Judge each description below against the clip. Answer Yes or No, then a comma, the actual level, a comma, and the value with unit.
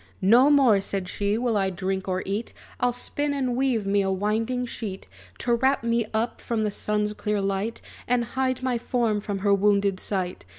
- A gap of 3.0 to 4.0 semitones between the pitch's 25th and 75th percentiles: Yes, average, 3.7 semitones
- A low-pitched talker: No, high, 215 Hz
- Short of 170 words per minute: No, average, 195 wpm